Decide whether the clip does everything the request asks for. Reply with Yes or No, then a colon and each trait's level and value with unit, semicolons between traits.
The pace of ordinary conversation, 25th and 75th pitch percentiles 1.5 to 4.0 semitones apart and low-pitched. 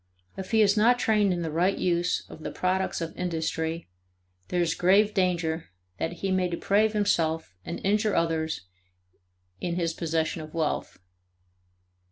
No: average, 155 wpm; average, 3.3 semitones; medium, 175 Hz